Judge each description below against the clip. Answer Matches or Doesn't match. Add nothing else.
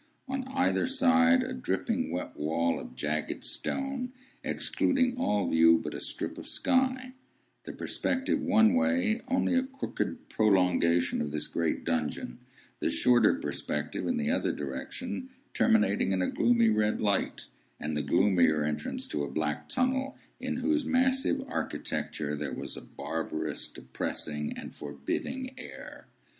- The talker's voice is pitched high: Matches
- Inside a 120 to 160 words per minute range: Matches